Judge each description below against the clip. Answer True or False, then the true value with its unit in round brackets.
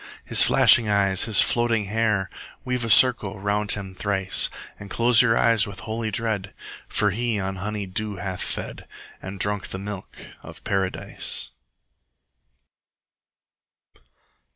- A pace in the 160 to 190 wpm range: False (135 wpm)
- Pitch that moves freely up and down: False (2.7 semitones)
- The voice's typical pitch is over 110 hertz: False (105 Hz)